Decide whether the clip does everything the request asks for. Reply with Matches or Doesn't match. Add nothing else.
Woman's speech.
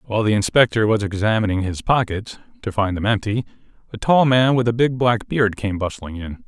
Doesn't match